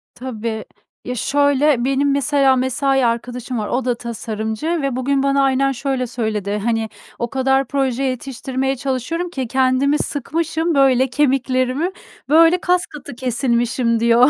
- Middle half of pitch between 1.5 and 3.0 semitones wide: Yes, narrow, 2.5 semitones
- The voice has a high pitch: Yes, very high, 260 Hz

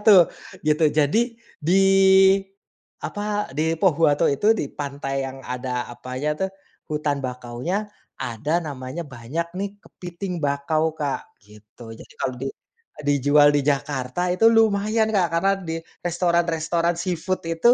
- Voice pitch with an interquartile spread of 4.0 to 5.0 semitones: Yes, average, 4.3 semitones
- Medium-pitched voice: Yes, medium, 150 Hz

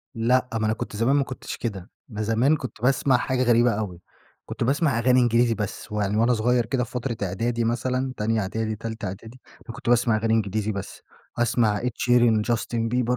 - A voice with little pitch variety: Yes, narrow, 2.3 semitones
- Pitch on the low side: Yes, low, 115 Hz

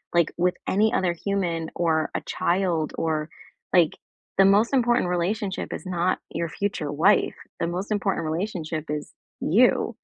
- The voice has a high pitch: No, medium, 175 Hz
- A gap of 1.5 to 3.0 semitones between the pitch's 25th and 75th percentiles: No, average, 3.4 semitones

